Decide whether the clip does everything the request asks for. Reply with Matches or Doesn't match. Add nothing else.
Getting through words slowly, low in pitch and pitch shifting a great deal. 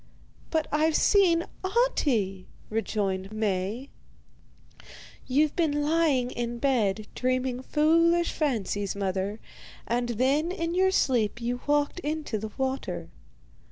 Doesn't match